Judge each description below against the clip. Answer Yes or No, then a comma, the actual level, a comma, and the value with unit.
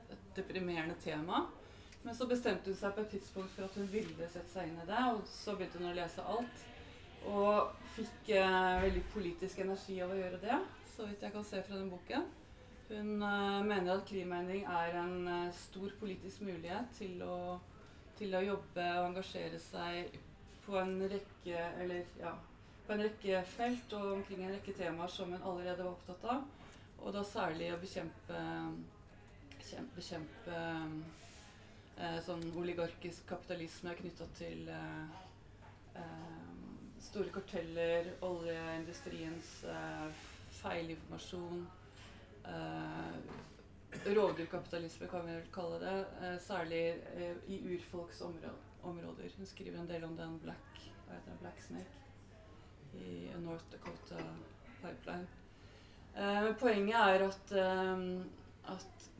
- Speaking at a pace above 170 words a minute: No, average, 140 wpm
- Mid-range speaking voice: Yes, medium, 175 Hz